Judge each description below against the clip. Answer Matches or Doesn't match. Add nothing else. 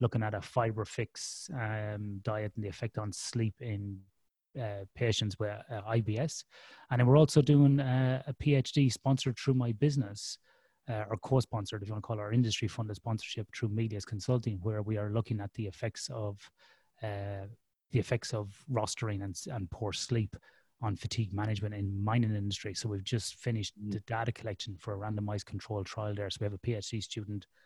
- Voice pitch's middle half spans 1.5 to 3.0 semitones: Matches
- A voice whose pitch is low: Matches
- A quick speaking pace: Doesn't match